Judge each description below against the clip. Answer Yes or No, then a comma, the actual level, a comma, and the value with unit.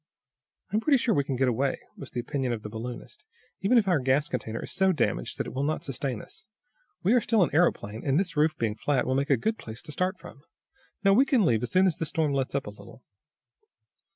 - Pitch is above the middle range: No, medium, 140 Hz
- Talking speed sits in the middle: No, fast, 250 wpm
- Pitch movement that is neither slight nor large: No, wide, 7.0 semitones